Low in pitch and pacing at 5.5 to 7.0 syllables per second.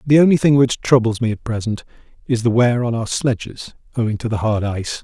Yes: low, 120 Hz; 5.8 syllables/s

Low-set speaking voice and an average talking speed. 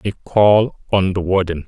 Yes: very low, 95 Hz; average, 180 wpm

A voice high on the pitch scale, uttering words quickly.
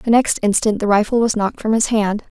Yes: high, 215 Hz; fast, 250 wpm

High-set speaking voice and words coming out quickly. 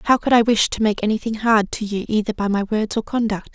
Yes: high, 215 Hz; fast, 270 wpm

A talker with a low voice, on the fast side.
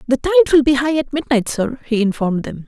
No: very high, 260 Hz; fast, 245 wpm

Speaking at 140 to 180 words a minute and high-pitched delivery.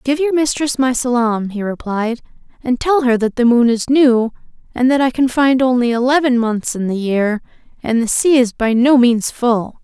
No: fast, 205 wpm; high, 245 Hz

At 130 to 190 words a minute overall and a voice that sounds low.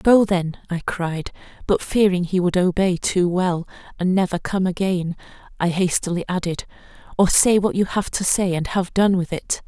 No: average, 180 wpm; medium, 185 Hz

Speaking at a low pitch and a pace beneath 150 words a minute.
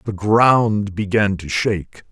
Yes: low, 105 Hz; average, 140 wpm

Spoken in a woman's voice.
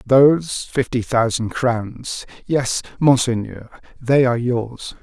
No: male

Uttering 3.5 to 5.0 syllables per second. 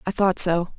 Yes: 4.9 syllables/s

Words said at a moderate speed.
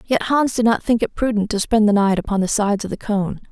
No: fast, 290 wpm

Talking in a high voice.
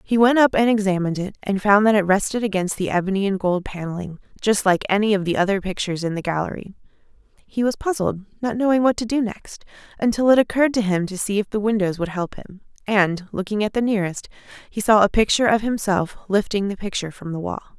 Yes: high, 205 Hz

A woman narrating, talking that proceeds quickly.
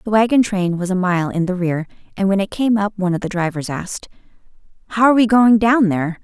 Yes: female; fast, 240 wpm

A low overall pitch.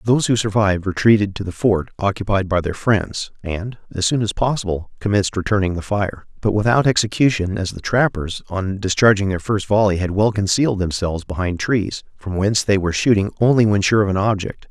Yes: low, 100 Hz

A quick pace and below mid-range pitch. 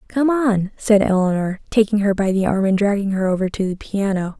No: fast, 220 wpm; high, 200 Hz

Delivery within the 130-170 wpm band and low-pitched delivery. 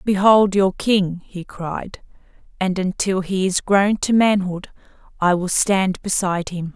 No: average, 150 wpm; high, 190 Hz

